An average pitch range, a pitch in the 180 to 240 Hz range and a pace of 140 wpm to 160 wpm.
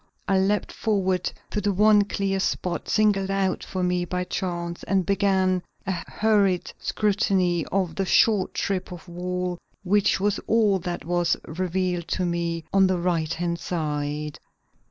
No: narrow, 2.1 semitones; medium, 185 Hz; average, 155 wpm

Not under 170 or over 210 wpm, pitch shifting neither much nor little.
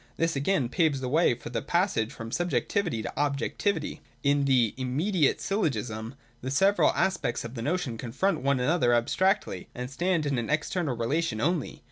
No: average, 175 wpm; wide, 6.3 semitones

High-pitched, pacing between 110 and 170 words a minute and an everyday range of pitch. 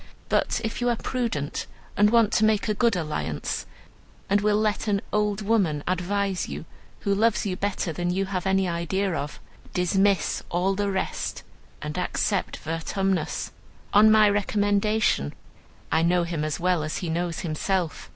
Yes: high, 195 Hz; average, 160 wpm; average, 3.3 semitones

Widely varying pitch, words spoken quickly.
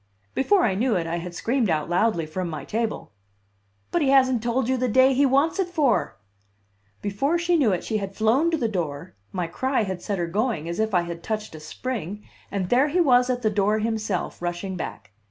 Yes: wide, 6.5 semitones; fast, 220 wpm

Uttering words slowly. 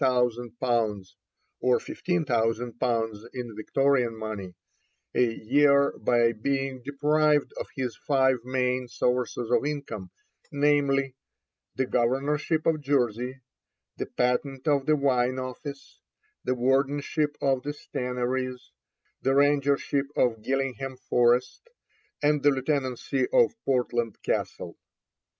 Yes: slow, 105 wpm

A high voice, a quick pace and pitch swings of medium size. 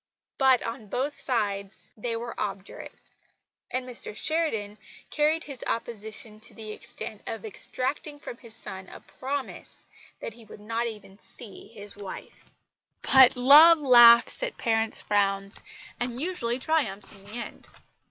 No: high, 235 Hz; average, 140 wpm; average, 3.9 semitones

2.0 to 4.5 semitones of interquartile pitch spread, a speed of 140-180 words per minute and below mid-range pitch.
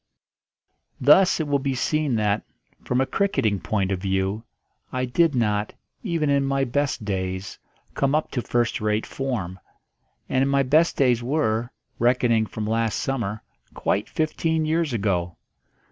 No: average, 4.9 semitones; average, 145 wpm; low, 125 Hz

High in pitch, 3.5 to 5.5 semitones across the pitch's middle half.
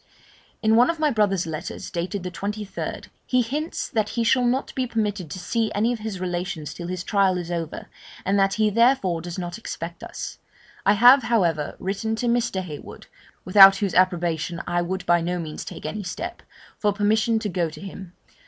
Yes: high, 195 Hz; average, 4.1 semitones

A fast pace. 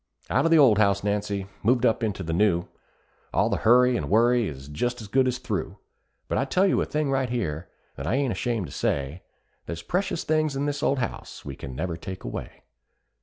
Yes: fast, 220 wpm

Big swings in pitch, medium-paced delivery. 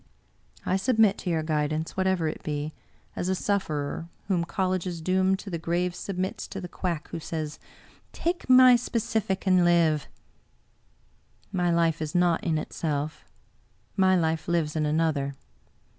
No: average, 3.1 semitones; average, 145 wpm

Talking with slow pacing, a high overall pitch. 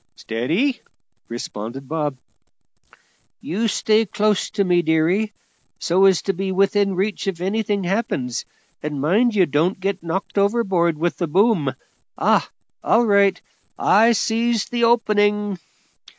Yes: slow, 125 wpm; high, 195 Hz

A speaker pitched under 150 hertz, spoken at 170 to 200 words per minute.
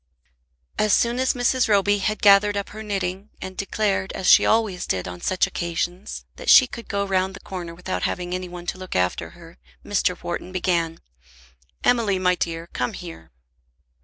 No: medium, 185 Hz; average, 180 wpm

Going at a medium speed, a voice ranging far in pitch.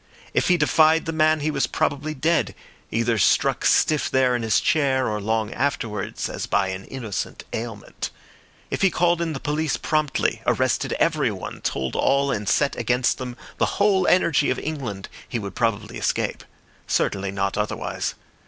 Yes: average, 165 wpm; wide, 6.3 semitones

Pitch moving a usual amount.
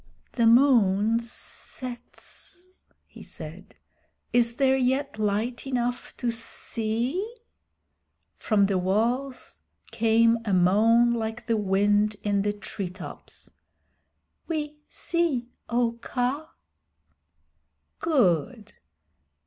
Yes: average, 3.5 semitones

